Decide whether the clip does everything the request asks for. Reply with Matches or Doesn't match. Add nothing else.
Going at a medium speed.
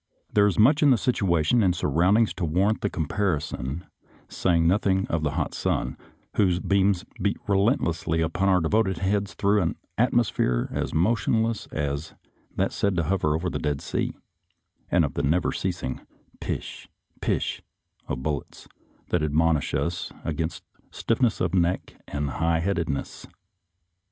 Matches